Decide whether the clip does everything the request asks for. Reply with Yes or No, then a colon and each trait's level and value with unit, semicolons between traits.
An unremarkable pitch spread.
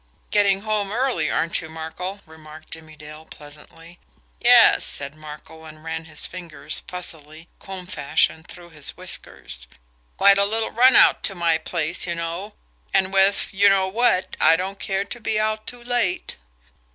Yes: average, 3.9 semitones